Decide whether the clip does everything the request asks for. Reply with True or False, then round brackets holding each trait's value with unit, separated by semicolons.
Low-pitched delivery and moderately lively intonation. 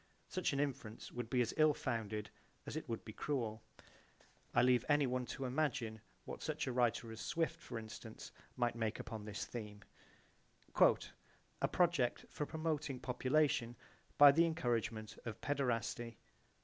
True (125 Hz; 4.3 semitones)